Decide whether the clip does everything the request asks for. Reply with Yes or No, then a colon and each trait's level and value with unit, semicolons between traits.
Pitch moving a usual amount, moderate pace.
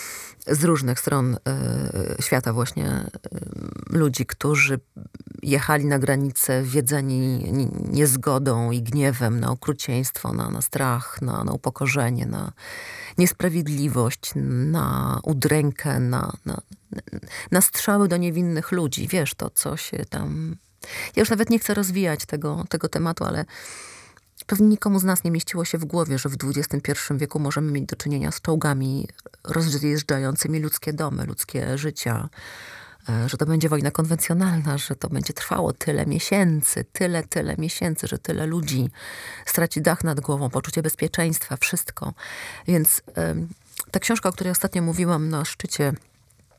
Yes: average, 4.1 semitones; average, 140 wpm